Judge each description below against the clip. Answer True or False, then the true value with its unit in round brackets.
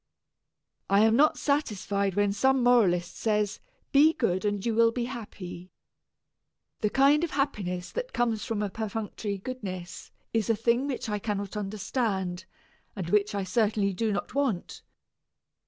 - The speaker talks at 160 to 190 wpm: False (150 wpm)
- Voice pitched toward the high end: True (210 Hz)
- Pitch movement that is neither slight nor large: True (3.6 semitones)